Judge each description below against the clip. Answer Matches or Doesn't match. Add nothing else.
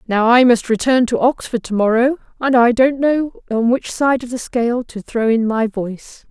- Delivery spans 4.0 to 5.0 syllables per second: Matches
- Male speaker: Doesn't match